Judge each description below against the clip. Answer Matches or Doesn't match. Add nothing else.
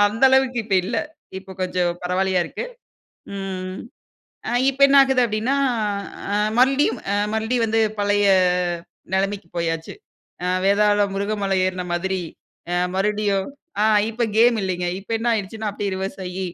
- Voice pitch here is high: Matches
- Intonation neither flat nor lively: Matches